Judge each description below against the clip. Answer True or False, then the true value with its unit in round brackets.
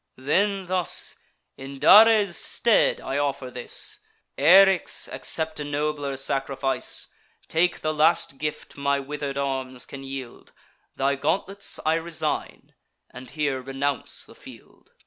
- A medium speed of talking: False (125 wpm)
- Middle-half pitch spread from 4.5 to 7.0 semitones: False (3.5 semitones)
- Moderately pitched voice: True (145 Hz)